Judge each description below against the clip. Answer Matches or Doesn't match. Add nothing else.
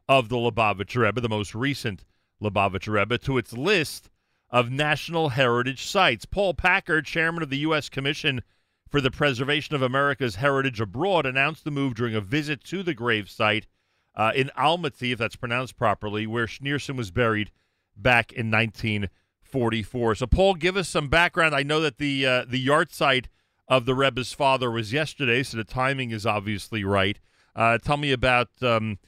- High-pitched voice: Doesn't match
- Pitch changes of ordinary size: Matches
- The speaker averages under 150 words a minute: Doesn't match